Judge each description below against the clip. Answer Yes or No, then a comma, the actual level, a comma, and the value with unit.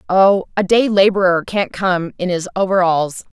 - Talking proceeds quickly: No, average, 160 wpm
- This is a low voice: No, medium, 185 Hz